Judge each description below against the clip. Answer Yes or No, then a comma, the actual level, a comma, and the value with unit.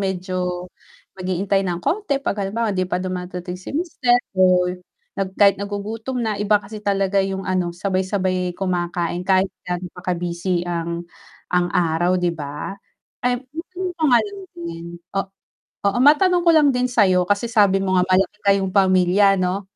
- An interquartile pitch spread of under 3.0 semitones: Yes, narrow, 2.5 semitones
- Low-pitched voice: No, high, 190 Hz